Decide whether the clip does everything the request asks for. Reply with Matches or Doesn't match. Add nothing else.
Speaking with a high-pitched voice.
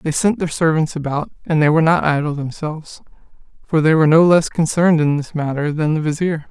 Doesn't match